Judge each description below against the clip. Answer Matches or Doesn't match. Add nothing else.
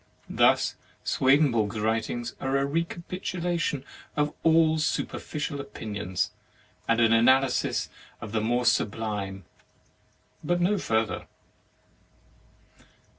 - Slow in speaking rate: Matches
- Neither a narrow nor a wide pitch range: Doesn't match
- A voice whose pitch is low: Matches